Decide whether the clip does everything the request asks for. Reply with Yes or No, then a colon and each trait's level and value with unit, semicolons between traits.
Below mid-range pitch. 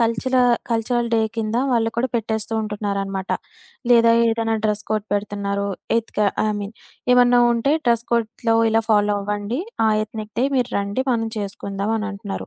No: high, 220 Hz